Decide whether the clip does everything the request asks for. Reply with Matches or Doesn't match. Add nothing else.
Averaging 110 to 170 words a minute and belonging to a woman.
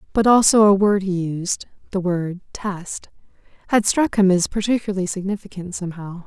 Matches